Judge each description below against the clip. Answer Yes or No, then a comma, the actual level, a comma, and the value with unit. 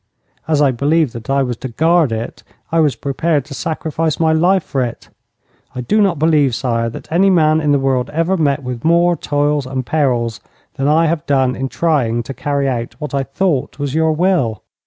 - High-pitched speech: No, medium, 145 Hz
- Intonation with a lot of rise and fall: No, average, 3.9 semitones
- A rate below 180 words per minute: No, fast, 205 wpm